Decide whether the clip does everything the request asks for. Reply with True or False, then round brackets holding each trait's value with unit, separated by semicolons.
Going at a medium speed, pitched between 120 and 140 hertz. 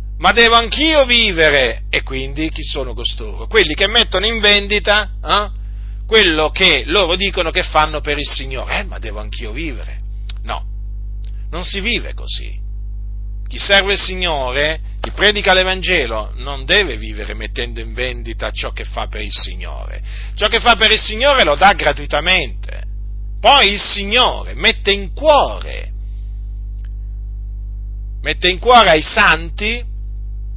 True (145 wpm; 135 Hz)